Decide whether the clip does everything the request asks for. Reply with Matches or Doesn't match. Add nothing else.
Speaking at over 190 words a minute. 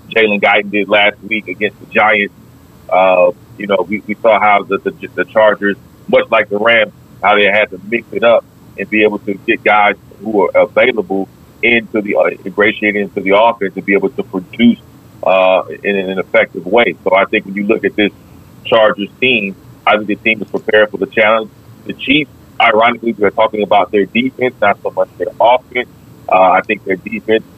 Matches